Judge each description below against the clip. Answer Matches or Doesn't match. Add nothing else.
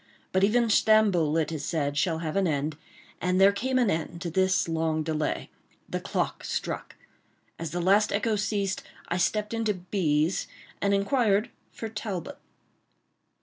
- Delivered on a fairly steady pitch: Doesn't match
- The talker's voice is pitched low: Doesn't match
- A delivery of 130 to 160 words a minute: Matches